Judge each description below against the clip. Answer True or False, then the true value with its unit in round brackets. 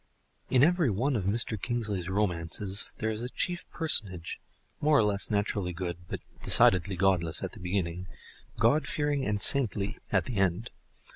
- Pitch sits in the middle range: False (105 Hz)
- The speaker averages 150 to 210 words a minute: True (160 wpm)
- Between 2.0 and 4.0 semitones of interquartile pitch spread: False (5.0 semitones)